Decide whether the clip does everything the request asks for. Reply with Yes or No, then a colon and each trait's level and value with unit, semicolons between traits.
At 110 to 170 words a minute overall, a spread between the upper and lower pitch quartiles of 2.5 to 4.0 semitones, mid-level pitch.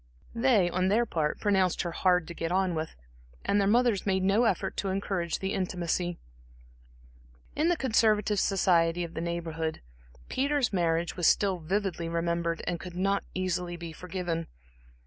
Yes: average, 160 wpm; average, 2.8 semitones; medium, 180 Hz